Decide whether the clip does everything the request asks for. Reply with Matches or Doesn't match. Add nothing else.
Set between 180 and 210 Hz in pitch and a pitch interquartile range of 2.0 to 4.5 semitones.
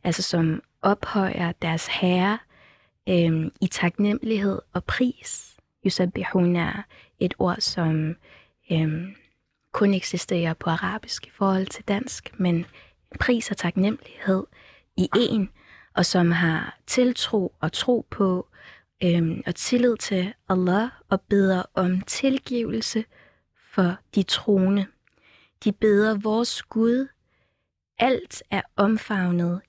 Matches